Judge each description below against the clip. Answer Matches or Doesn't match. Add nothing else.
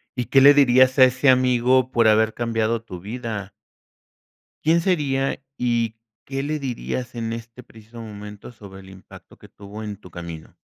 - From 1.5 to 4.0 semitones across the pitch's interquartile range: Matches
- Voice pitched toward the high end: Doesn't match